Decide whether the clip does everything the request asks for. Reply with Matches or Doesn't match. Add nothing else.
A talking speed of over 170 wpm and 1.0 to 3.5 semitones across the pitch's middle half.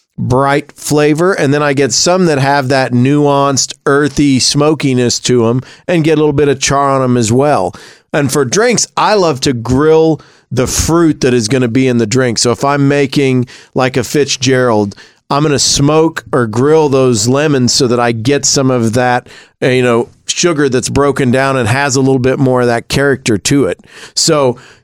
Matches